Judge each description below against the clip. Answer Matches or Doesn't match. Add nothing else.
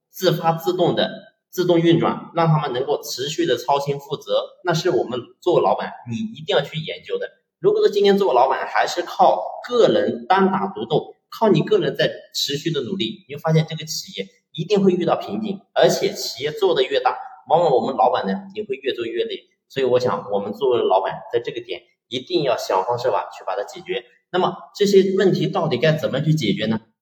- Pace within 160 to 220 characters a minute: Doesn't match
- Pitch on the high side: Matches